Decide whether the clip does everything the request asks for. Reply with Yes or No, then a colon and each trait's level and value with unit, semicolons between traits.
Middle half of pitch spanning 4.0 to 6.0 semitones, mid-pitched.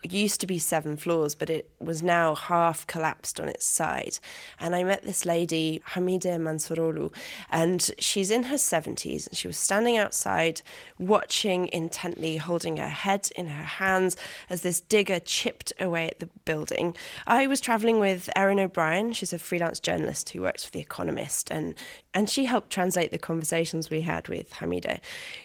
No: average, 3.5 semitones; medium, 180 Hz